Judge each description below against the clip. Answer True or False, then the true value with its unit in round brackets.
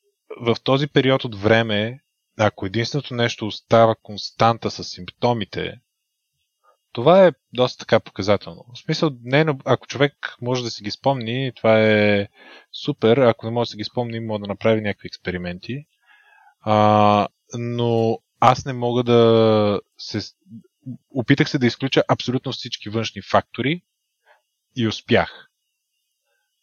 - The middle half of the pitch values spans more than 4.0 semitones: False (3.7 semitones)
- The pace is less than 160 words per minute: True (135 wpm)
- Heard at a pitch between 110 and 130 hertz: True (120 Hz)